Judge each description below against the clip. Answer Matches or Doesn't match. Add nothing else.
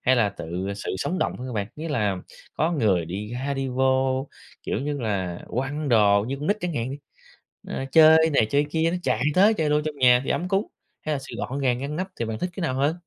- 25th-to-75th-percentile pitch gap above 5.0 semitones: Matches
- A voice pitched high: Doesn't match